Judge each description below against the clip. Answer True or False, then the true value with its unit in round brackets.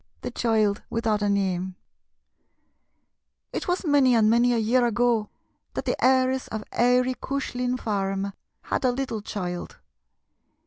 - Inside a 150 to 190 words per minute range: False (135 wpm)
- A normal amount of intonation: True (3.4 semitones)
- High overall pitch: True (230 Hz)